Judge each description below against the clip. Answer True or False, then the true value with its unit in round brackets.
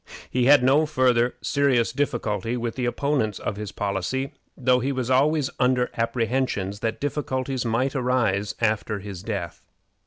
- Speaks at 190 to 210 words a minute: False (150 wpm)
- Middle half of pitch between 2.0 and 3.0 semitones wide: False (3.4 semitones)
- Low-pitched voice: True (125 Hz)